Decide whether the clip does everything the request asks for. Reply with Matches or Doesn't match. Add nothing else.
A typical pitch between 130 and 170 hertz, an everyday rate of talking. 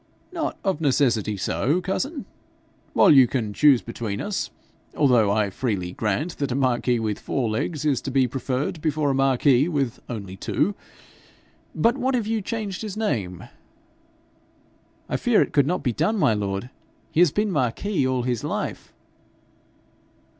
Matches